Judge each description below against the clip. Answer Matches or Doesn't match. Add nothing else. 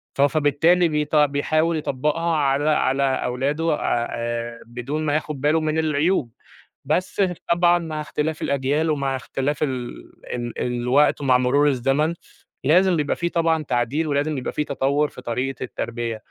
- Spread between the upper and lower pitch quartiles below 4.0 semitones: Matches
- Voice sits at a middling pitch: Matches